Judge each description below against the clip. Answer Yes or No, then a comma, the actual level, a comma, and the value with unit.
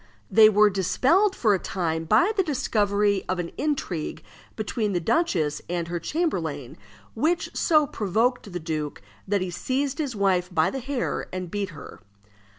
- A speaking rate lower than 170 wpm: Yes, average, 160 wpm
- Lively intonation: Yes, wide, 6.8 semitones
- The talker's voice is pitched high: Yes, high, 205 Hz